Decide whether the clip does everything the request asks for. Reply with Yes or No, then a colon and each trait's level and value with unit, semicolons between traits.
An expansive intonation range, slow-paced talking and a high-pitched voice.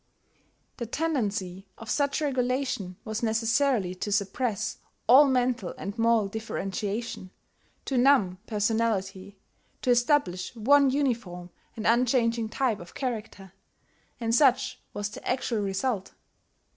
No: average, 4.1 semitones; slow, 115 wpm; high, 225 Hz